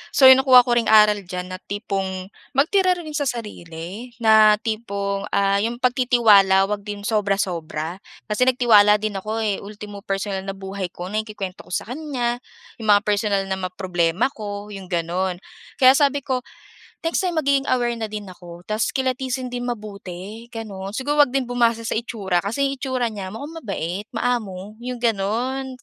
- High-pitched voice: Yes, high, 215 Hz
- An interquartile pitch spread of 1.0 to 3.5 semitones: No, average, 4.1 semitones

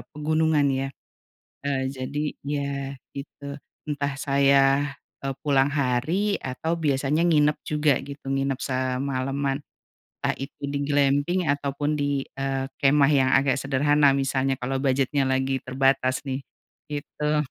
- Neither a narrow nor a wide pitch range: No, narrow, 1.6 semitones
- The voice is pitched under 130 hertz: No, medium, 140 Hz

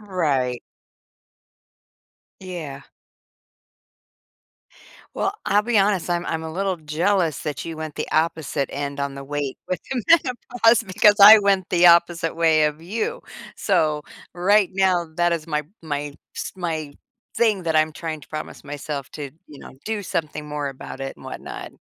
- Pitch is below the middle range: No, medium, 165 Hz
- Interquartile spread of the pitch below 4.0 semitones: No, average, 4.3 semitones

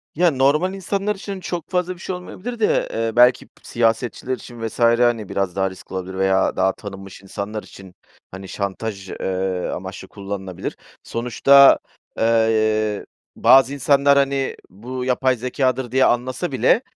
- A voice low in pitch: Yes, low, 120 Hz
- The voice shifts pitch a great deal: Yes, wide, 5.7 semitones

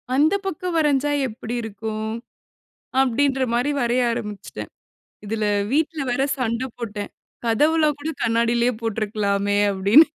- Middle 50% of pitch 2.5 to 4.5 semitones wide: No, average, 4.9 semitones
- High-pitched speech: Yes, high, 235 Hz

